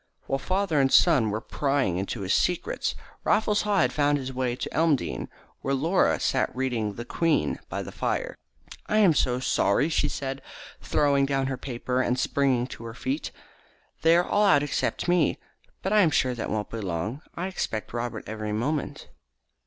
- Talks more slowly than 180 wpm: No, average, 185 wpm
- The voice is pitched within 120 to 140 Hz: Yes, low, 135 Hz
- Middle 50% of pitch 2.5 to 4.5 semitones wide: No, average, 5.3 semitones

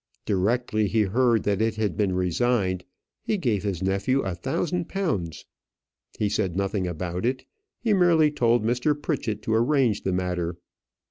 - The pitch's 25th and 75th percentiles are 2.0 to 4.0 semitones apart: No, average, 5.3 semitones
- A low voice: Yes, low, 110 Hz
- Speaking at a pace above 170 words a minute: No, average, 155 wpm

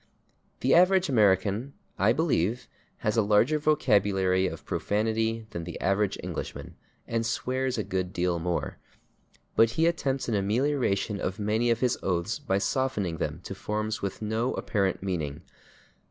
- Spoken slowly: No, average, 150 wpm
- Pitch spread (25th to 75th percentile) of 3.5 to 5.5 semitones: Yes, average, 4.5 semitones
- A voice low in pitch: Yes, low, 105 Hz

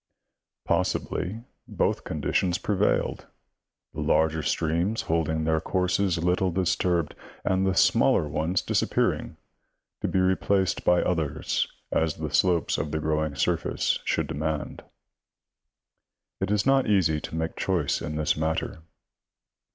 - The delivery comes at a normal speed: No, slow, 130 wpm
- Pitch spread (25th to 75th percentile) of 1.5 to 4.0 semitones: Yes, average, 3.0 semitones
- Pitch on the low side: Yes, very low, 85 Hz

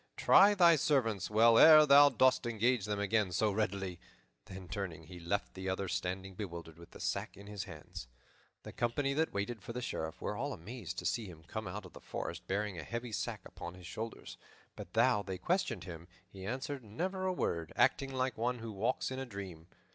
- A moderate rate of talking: No, fast, 210 wpm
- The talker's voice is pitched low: Yes, low, 105 Hz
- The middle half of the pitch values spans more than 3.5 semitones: Yes, average, 5.3 semitones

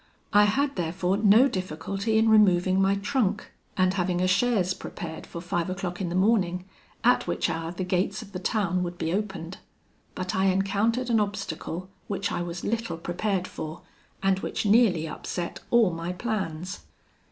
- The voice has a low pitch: No, high, 190 Hz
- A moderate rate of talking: Yes, average, 170 wpm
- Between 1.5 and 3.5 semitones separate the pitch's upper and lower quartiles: Yes, average, 2.9 semitones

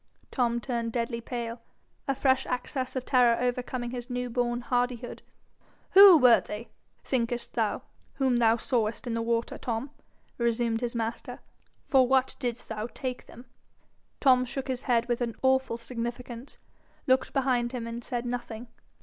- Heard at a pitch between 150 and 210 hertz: No, high, 245 Hz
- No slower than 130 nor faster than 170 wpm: Yes, average, 155 wpm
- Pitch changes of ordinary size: No, narrow, 1.6 semitones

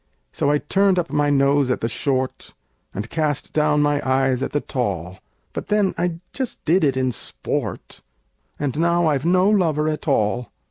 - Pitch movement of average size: Yes, average, 4.3 semitones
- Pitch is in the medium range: Yes, medium, 145 Hz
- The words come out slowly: No, average, 180 wpm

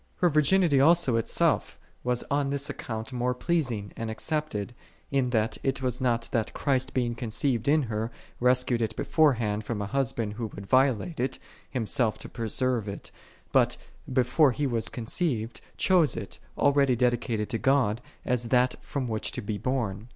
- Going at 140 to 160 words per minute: No, average, 170 wpm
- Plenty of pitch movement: No, average, 3.4 semitones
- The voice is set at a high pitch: No, low, 125 Hz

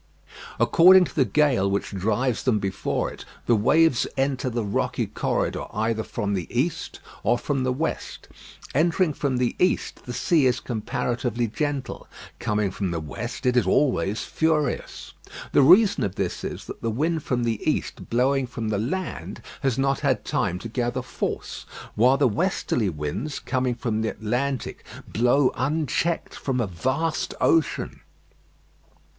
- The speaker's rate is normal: Yes, average, 155 wpm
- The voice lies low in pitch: Yes, low, 125 Hz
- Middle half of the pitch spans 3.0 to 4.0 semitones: No, average, 4.5 semitones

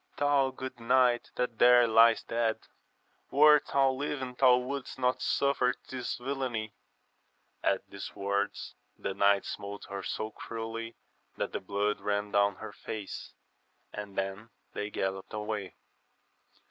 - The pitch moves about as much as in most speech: Yes, average, 3.9 semitones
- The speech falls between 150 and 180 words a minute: No, slow, 135 wpm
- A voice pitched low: Yes, low, 115 Hz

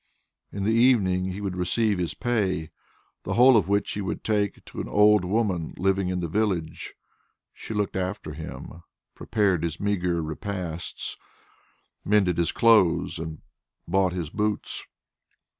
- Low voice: Yes, very low, 95 Hz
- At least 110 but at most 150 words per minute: Yes, average, 145 wpm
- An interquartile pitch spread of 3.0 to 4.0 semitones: Yes, average, 3.3 semitones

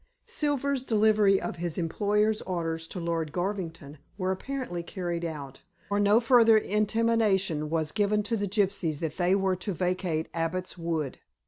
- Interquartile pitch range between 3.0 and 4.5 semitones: Yes, average, 4.1 semitones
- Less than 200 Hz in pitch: Yes, medium, 185 Hz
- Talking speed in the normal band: Yes, average, 150 wpm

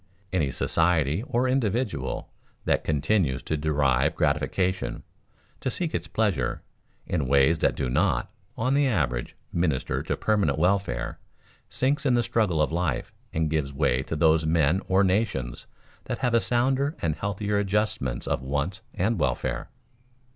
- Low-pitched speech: Yes, very low, 85 Hz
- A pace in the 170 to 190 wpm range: No, average, 145 wpm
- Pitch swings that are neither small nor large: No, wide, 7.1 semitones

